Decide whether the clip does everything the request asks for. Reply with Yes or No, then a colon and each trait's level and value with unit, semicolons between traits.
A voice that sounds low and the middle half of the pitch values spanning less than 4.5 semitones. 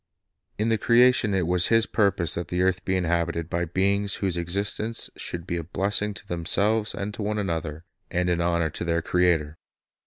Yes: very low, 90 Hz; average, 3.2 semitones